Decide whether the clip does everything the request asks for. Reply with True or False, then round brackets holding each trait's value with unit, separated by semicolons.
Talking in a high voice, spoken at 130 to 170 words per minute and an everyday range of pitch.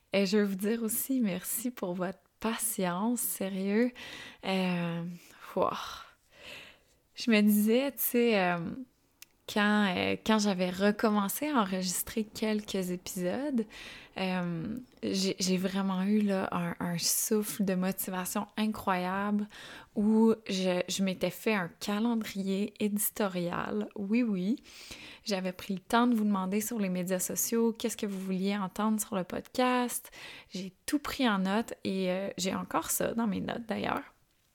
True (205 Hz; 145 wpm; 3.3 semitones)